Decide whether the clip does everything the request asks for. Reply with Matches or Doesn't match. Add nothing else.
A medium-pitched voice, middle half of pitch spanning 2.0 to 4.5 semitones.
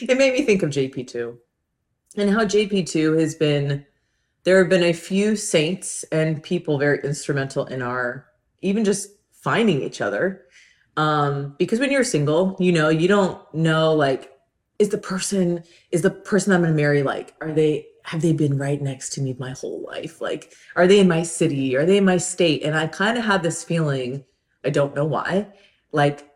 Doesn't match